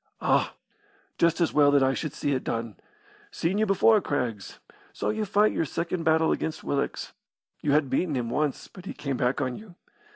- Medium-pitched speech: Yes, medium, 150 Hz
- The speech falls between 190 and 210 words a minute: Yes, average, 195 wpm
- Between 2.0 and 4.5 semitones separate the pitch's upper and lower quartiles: No, average, 5.1 semitones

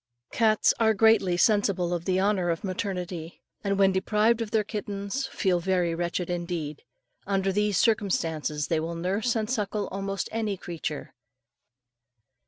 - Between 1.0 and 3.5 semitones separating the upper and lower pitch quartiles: Yes, average, 3.2 semitones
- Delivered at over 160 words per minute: No, average, 145 wpm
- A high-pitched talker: Yes, high, 195 Hz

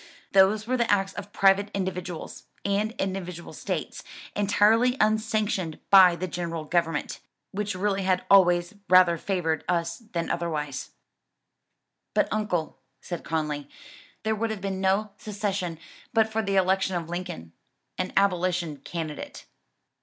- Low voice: No, high, 190 Hz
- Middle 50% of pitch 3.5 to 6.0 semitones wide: No, average, 3.1 semitones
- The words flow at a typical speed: No, slow, 130 wpm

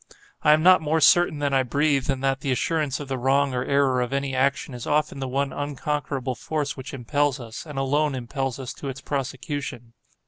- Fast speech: Yes, fast, 210 wpm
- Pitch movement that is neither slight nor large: No, narrow, 1.9 semitones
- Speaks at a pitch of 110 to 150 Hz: Yes, medium, 140 Hz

